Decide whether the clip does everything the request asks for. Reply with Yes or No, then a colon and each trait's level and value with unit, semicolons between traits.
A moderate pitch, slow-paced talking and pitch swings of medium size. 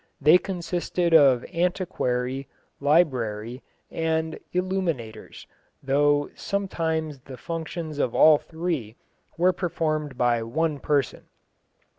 Yes: medium, 155 Hz; slow, 95 wpm; average, 4.4 semitones